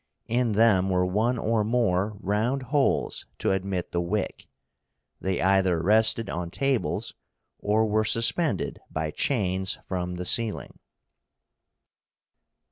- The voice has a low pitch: Yes, low, 105 Hz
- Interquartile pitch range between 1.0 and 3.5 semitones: No, average, 3.9 semitones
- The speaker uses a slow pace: Yes, slow, 120 wpm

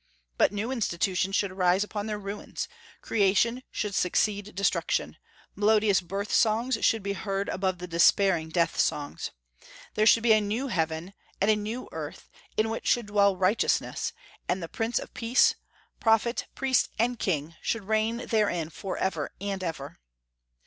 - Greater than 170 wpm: No, average, 155 wpm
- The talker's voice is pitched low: No, high, 200 Hz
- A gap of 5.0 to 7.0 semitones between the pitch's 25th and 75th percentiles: No, average, 3.1 semitones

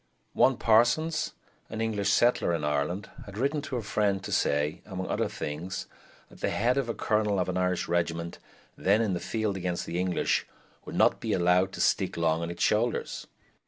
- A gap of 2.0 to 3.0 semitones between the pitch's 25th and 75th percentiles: No, average, 4.3 semitones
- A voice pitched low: Yes, very low, 95 Hz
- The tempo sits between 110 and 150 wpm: No, average, 195 wpm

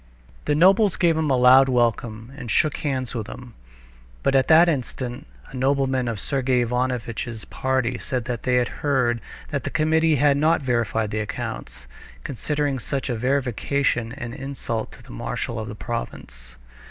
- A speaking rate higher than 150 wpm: Yes, average, 165 wpm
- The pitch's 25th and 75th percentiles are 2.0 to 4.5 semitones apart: Yes, average, 3.1 semitones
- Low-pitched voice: Yes, low, 130 Hz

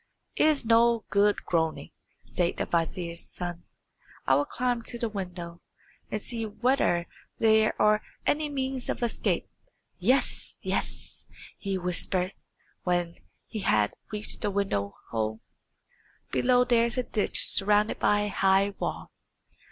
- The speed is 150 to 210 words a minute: No, slow, 135 wpm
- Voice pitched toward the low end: No, high, 205 Hz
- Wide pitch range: No, average, 5.0 semitones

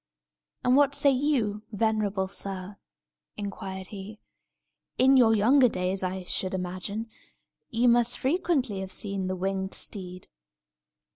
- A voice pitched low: No, high, 205 Hz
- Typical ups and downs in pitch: Yes, average, 4.3 semitones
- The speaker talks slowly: Yes, slow, 125 wpm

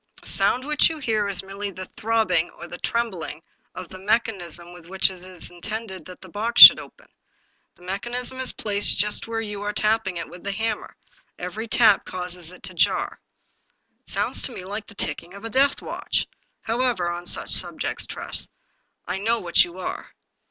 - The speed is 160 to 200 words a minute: Yes, average, 195 wpm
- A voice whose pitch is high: Yes, high, 200 Hz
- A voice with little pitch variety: No, average, 3.9 semitones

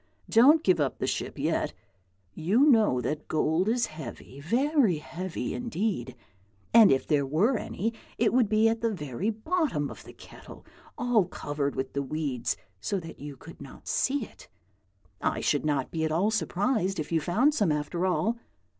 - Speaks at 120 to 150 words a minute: No, average, 175 wpm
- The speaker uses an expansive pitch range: Yes, wide, 7.3 semitones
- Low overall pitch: No, medium, 185 Hz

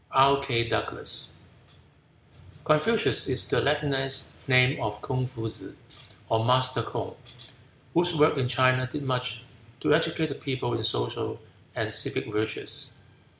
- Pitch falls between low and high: No, low, 130 Hz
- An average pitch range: Yes, average, 3.7 semitones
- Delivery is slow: Yes, slow, 125 wpm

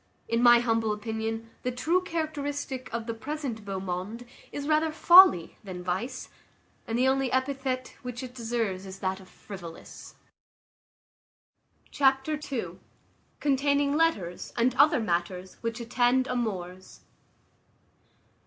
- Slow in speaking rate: Yes, slow, 125 wpm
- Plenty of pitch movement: No, average, 4.9 semitones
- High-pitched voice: Yes, high, 240 Hz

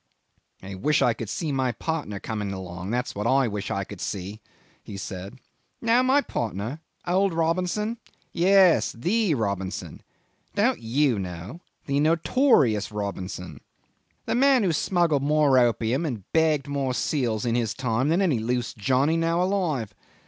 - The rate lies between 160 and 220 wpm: No, average, 150 wpm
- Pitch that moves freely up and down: Yes, wide, 7.9 semitones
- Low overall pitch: Yes, low, 130 Hz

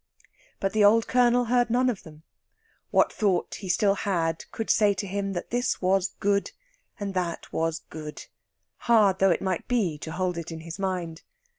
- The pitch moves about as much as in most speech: Yes, average, 4.0 semitones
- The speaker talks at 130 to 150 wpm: No, average, 180 wpm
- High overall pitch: Yes, high, 195 Hz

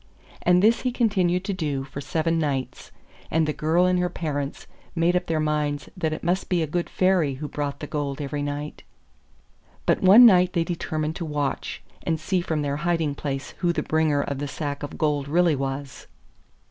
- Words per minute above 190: Yes, average, 200 wpm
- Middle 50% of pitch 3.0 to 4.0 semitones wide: Yes, average, 3.4 semitones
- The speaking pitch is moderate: Yes, medium, 155 Hz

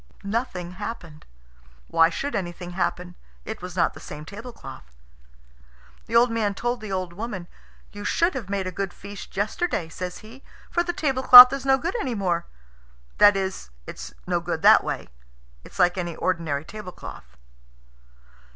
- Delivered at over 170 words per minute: No, average, 160 wpm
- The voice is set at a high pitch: Yes, high, 200 Hz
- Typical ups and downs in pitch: Yes, average, 4.8 semitones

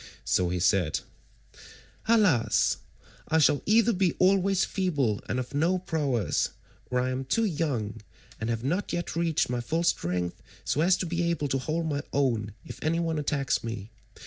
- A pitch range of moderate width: No, wide, 6.6 semitones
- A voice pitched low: No, medium, 145 Hz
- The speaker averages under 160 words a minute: No, average, 170 wpm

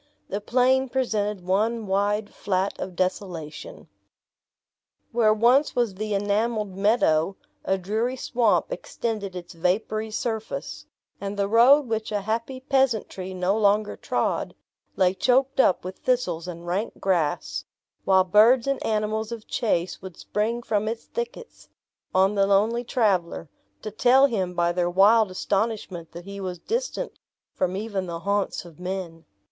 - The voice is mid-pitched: No, high, 205 Hz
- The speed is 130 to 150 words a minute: Yes, average, 145 wpm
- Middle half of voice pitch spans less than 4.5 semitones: Yes, average, 3.8 semitones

